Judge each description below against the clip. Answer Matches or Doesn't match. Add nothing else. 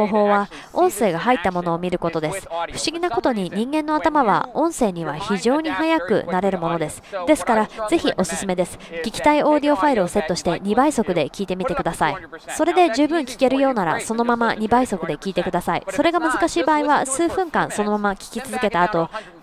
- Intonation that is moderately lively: Doesn't match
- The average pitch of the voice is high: Matches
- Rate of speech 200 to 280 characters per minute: Doesn't match